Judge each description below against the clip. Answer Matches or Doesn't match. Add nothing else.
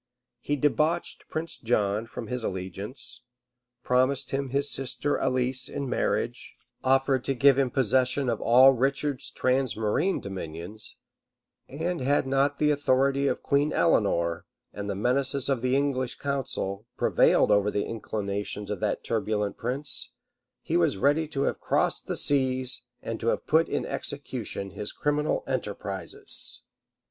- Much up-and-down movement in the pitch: Doesn't match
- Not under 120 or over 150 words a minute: Matches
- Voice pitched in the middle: Doesn't match